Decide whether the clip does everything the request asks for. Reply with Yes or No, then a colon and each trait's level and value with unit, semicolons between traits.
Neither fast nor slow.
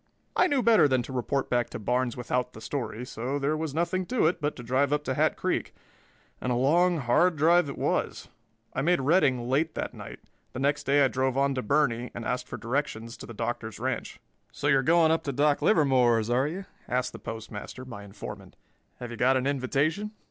No: fast, 215 wpm